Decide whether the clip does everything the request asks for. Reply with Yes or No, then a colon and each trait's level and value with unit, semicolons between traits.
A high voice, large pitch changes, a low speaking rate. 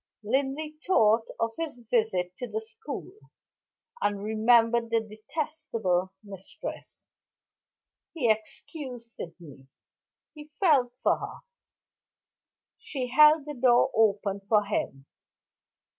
Yes: high, 230 Hz; wide, 5.7 semitones; slow, 100 wpm